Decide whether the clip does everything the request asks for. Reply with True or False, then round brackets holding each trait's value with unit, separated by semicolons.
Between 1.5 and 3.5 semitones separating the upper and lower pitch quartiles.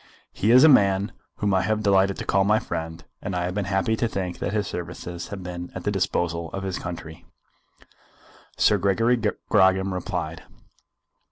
True (2.6 semitones)